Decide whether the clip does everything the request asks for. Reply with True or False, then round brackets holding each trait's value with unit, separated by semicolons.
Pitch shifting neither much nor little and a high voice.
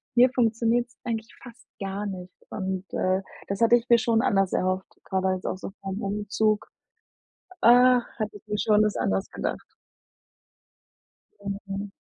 True (3.0 semitones; 210 Hz)